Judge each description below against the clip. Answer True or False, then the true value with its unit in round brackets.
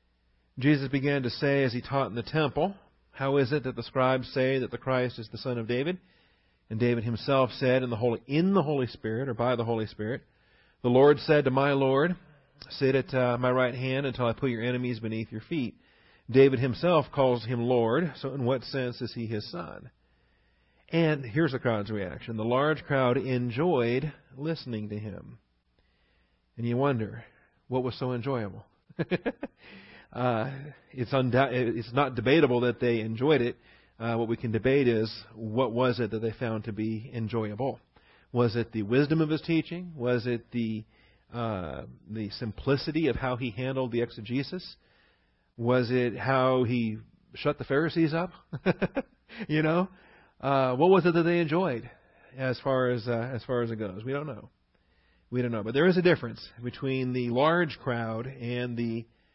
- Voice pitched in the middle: False (125 Hz)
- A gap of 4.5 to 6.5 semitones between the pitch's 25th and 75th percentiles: False (3.4 semitones)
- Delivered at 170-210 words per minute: True (180 wpm)